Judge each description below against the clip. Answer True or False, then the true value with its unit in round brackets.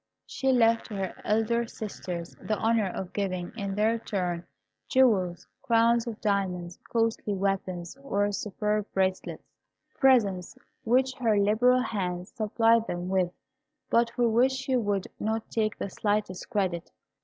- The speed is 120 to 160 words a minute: True (140 wpm)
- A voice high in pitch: True (210 Hz)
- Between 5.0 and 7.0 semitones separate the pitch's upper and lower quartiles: False (3.5 semitones)